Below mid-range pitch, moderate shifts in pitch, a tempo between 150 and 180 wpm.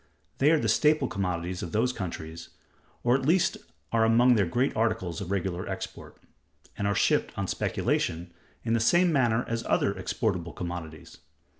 No: low, 110 Hz; wide, 5.8 semitones; average, 165 wpm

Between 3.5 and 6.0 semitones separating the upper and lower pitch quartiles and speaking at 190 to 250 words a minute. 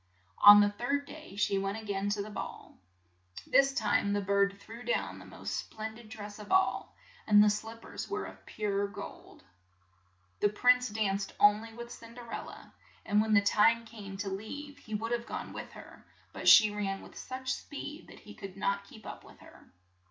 No: narrow, 2.6 semitones; fast, 205 wpm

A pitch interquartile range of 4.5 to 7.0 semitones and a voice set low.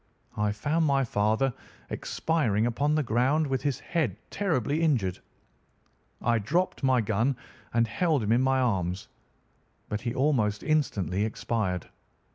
Yes: wide, 5.5 semitones; low, 120 Hz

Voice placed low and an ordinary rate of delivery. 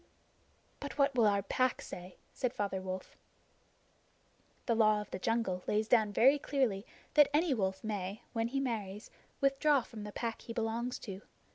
No: high, 225 Hz; average, 165 wpm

